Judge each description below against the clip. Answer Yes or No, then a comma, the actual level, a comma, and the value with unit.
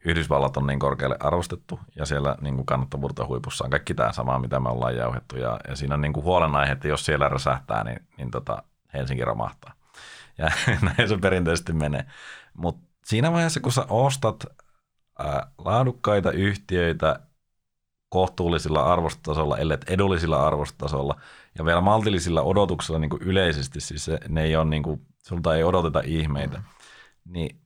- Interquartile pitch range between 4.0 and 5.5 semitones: Yes, average, 5.1 semitones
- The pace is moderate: Yes, average, 135 wpm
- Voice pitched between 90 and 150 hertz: No, very low, 80 Hz